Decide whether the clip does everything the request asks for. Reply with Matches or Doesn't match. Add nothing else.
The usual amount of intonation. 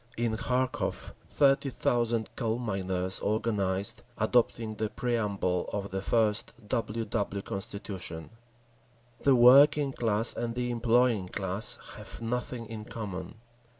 Matches